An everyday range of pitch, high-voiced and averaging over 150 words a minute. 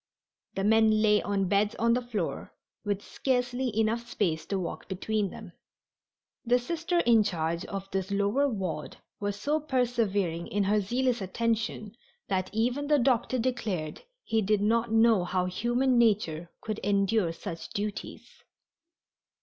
No: average, 3.6 semitones; high, 215 Hz; average, 145 wpm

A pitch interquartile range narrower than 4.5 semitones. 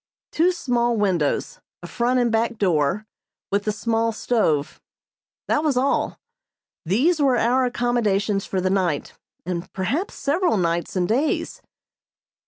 No: average, 5.0 semitones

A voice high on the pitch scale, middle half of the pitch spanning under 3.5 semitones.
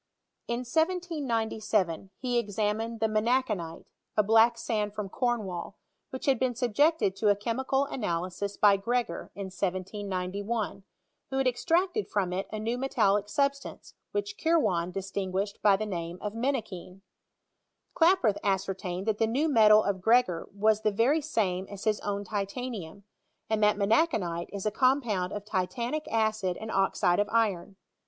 No: high, 210 Hz; average, 3.8 semitones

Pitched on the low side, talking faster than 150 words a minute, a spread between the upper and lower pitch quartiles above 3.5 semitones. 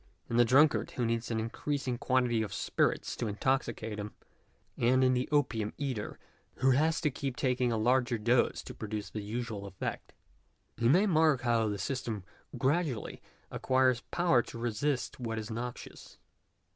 No: low, 120 Hz; average, 165 wpm; average, 2.9 semitones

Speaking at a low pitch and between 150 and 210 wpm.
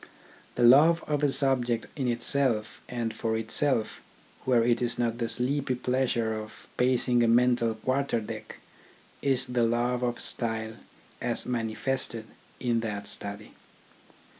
No: low, 120 Hz; average, 140 wpm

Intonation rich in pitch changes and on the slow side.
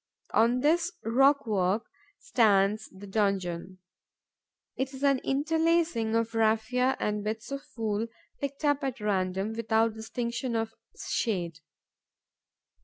No: average, 4.4 semitones; slow, 110 wpm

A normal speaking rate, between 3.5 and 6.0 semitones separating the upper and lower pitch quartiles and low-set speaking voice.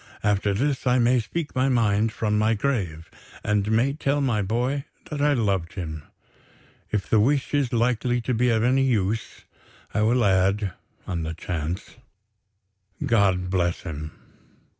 Yes: average, 155 wpm; average, 4.7 semitones; low, 110 Hz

